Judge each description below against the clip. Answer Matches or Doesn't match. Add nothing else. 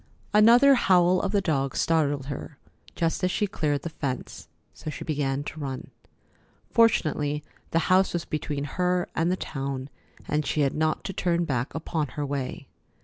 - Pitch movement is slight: Doesn't match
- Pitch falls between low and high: Matches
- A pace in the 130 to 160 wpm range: Doesn't match